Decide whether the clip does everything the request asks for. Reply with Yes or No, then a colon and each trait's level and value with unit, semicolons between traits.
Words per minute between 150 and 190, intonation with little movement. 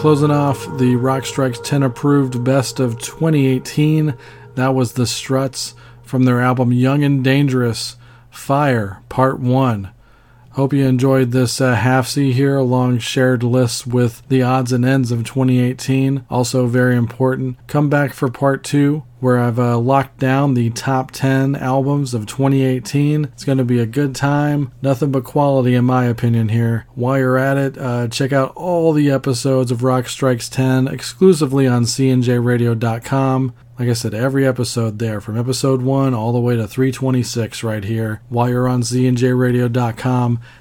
Yes: average, 165 wpm; narrow, 1.8 semitones